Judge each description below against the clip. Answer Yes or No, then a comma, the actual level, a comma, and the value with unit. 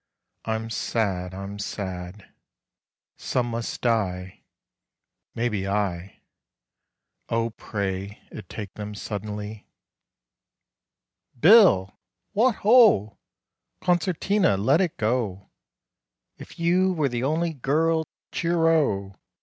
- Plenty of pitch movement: Yes, wide, 8.6 semitones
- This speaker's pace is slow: Yes, slow, 90 wpm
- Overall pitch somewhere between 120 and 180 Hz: No, low, 110 Hz